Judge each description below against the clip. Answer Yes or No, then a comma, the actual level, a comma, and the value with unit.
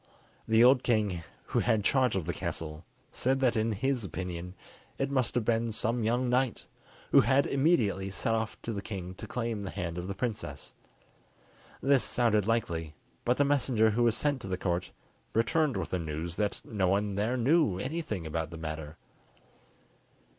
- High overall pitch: No, low, 110 Hz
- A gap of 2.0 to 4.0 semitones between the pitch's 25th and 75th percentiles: No, average, 5.2 semitones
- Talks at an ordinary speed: Yes, average, 180 wpm